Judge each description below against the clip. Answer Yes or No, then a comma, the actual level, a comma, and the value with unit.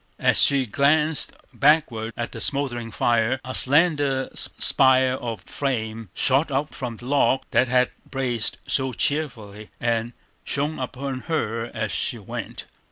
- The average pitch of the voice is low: Yes, low, 130 Hz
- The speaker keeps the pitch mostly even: No, average, 3.4 semitones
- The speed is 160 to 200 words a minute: No, average, 140 wpm